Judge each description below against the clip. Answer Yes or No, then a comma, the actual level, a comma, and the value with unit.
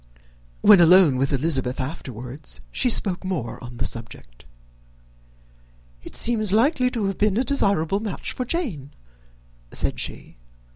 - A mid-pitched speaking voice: Yes, medium, 180 Hz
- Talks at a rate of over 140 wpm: No, slow, 135 wpm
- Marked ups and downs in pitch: Yes, wide, 8.5 semitones